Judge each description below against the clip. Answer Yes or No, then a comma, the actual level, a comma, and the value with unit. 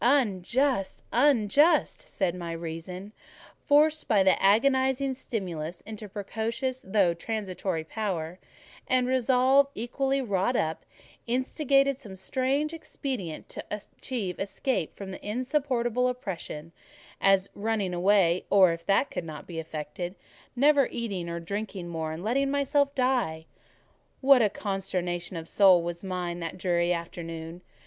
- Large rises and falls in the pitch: Yes, wide, 6.7 semitones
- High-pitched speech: Yes, high, 200 Hz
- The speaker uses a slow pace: Yes, slow, 125 wpm